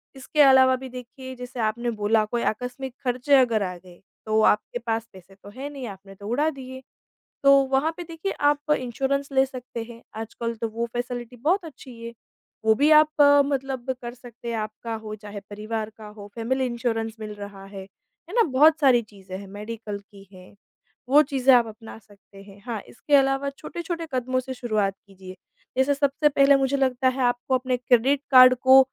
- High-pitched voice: Yes, high, 245 Hz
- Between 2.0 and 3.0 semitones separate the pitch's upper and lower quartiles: No, average, 3.7 semitones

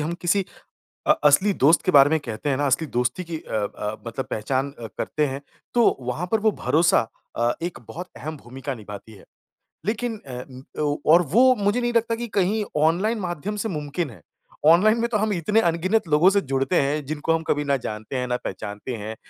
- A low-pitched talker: No, medium, 155 Hz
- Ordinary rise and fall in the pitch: No, wide, 6.4 semitones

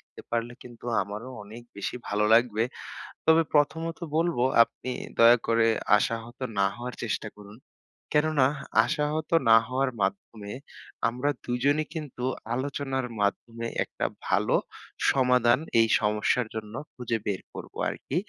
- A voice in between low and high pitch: No, low, 120 Hz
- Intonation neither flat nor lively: Yes, average, 3.5 semitones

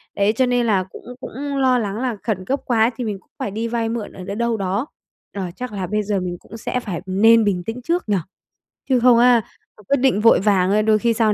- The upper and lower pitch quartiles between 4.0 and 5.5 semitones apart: No, average, 3.2 semitones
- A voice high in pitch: Yes, high, 220 Hz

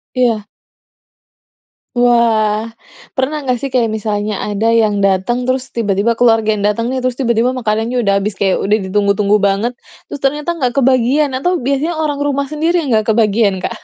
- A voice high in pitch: Yes, high, 230 Hz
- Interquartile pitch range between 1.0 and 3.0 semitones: No, average, 3.9 semitones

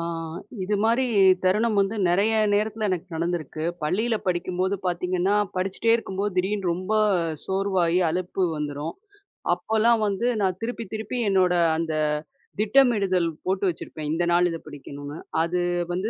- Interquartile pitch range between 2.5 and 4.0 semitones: Yes, average, 3.3 semitones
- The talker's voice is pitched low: No, medium, 185 Hz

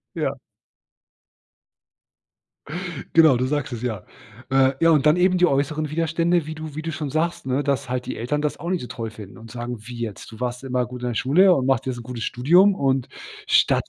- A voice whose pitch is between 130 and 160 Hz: Yes, low, 135 Hz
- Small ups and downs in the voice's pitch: No, average, 4.3 semitones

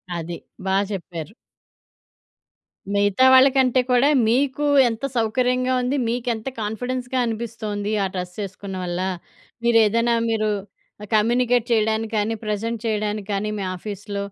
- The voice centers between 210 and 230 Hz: Yes, high, 220 Hz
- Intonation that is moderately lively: Yes, average, 3.2 semitones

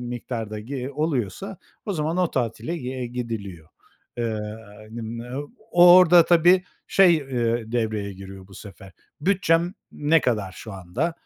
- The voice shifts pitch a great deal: Yes, wide, 7.2 semitones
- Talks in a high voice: No, low, 125 Hz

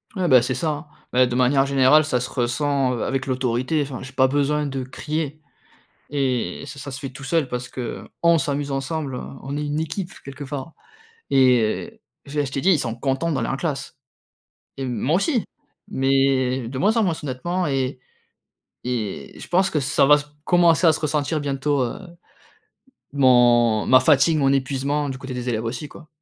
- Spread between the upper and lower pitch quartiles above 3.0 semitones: No, average, 2.7 semitones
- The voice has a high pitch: No, low, 135 Hz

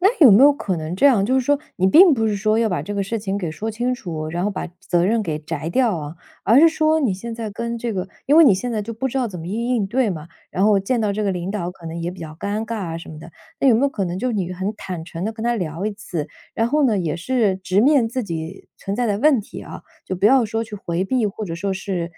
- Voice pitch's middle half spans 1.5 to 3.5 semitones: No, average, 4.7 semitones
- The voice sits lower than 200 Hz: No, high, 205 Hz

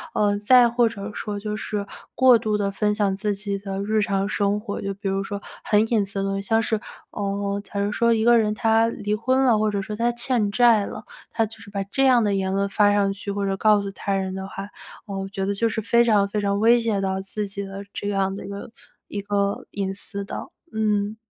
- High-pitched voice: Yes, high, 205 Hz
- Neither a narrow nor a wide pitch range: No, narrow, 1.7 semitones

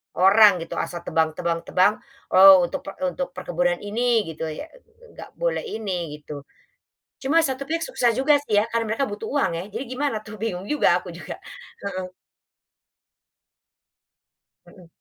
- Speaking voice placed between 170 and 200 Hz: No, high, 210 Hz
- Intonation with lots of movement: Yes, wide, 6.5 semitones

